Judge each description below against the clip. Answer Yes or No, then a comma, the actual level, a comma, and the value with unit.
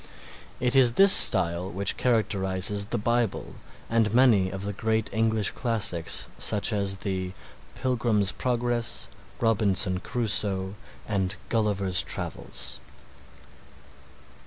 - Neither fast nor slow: No, slow, 105 wpm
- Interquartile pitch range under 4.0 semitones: Yes, average, 3.4 semitones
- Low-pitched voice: Yes, low, 105 Hz